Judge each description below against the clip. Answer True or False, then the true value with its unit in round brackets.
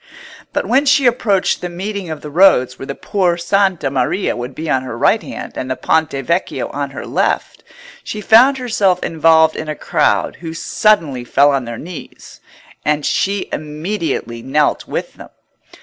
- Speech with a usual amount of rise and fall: False (6.1 semitones)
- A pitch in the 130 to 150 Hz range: False (160 Hz)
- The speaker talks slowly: False (175 wpm)